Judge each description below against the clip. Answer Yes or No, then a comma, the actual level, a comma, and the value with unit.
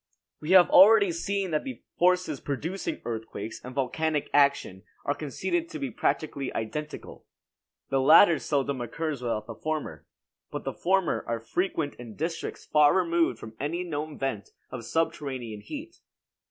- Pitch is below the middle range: No, medium, 150 Hz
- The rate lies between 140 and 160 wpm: Yes, average, 150 wpm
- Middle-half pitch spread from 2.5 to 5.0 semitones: No, wide, 5.5 semitones